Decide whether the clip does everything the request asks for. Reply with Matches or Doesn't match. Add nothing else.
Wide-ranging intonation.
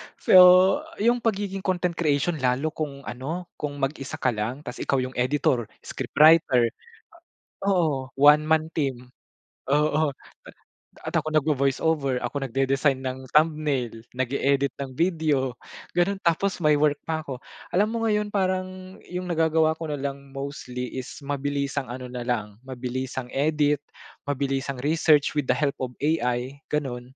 Doesn't match